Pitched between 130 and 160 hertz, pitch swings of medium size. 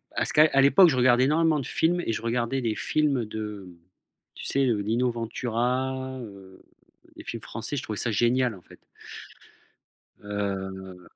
No: low, 120 Hz; average, 3.9 semitones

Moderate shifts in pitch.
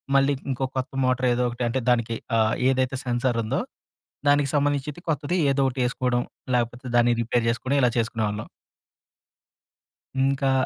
No: narrow, 2.3 semitones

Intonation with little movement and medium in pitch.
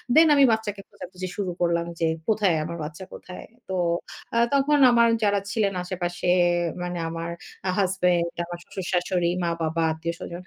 No: average, 3.0 semitones; medium, 180 Hz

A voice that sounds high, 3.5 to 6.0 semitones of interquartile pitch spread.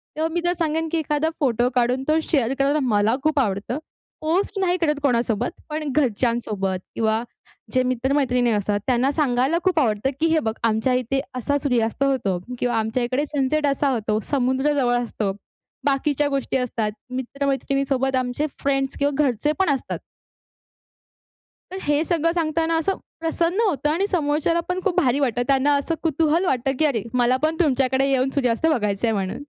Yes: very high, 270 Hz; average, 4.0 semitones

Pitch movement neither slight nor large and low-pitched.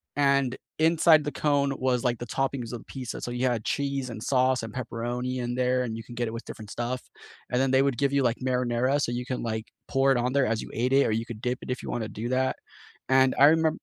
No: narrow, 2.2 semitones; low, 125 Hz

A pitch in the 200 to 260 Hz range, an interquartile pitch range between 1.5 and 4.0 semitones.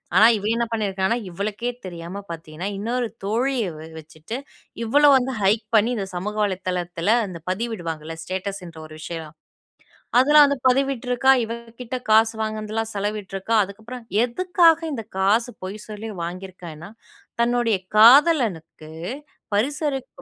No: high, 215 Hz; average, 4.7 semitones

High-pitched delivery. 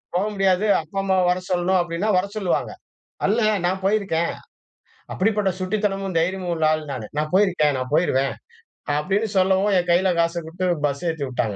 No: medium, 180 Hz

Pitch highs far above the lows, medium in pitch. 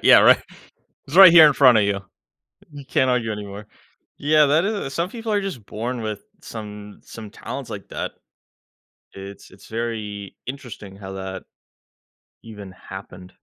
No: wide, 6.1 semitones; low, 115 Hz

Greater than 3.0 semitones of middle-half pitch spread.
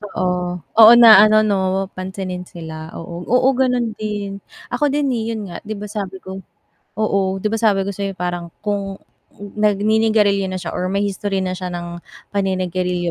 No: narrow, 2.6 semitones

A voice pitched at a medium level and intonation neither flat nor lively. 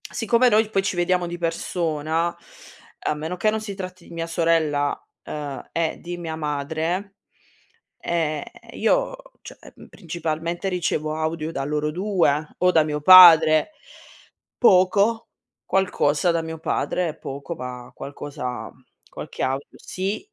Yes: medium, 165 Hz; average, 3.3 semitones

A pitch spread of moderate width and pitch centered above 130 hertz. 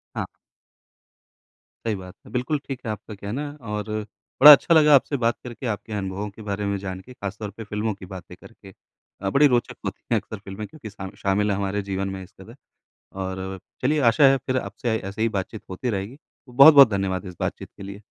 No: average, 4.2 semitones; low, 105 Hz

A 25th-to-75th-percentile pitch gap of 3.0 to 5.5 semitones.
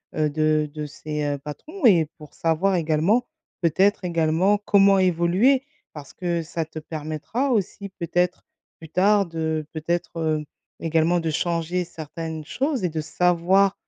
Yes: average, 3.4 semitones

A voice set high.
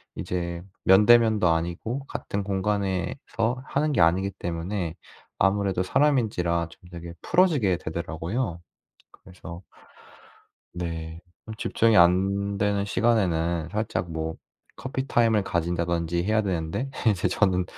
No: very low, 95 Hz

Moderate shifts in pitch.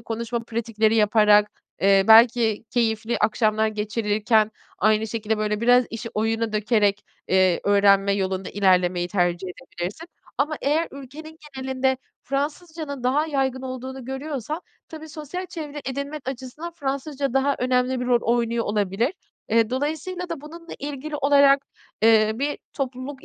Yes: average, 4.7 semitones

